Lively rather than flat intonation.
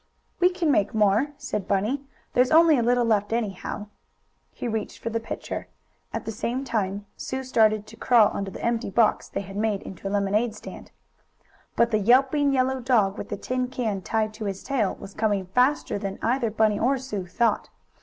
No: average, 3.7 semitones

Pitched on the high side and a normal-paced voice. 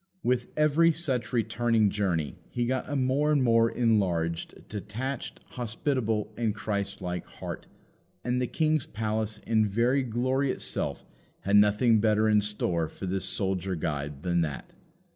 No: low, 110 Hz; average, 145 wpm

